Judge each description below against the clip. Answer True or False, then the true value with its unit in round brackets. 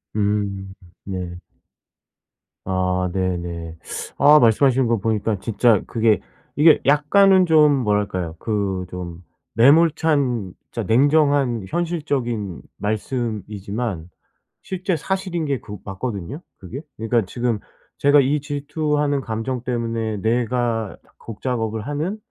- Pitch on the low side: True (115 Hz)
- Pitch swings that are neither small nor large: False (5.9 semitones)